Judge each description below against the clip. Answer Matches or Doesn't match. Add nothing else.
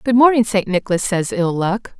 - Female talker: Matches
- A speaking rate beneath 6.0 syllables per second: Matches